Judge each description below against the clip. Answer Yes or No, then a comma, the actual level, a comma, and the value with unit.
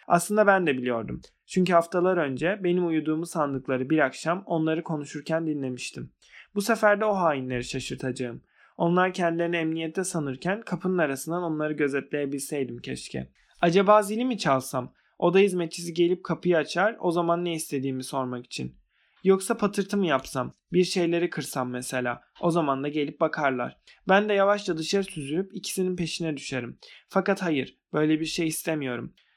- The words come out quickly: Yes, fast, 150 wpm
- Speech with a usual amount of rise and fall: Yes, average, 4.8 semitones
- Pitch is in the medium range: Yes, medium, 165 Hz